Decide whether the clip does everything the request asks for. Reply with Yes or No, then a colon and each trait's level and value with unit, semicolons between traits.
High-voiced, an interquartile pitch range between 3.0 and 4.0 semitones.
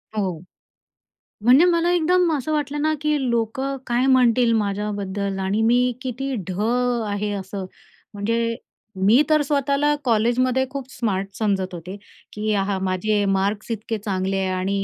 No: high, 225 Hz; average, 5.0 semitones